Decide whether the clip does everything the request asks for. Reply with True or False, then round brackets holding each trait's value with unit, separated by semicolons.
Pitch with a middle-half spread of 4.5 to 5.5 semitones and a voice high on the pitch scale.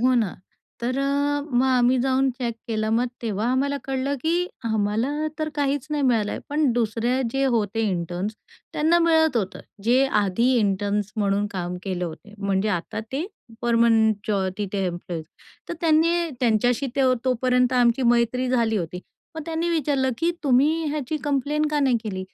True (4.9 semitones; 245 Hz)